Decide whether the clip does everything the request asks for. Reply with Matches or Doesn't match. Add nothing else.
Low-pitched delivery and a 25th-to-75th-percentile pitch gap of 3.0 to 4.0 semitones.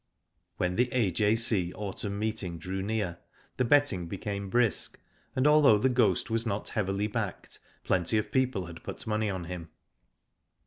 Matches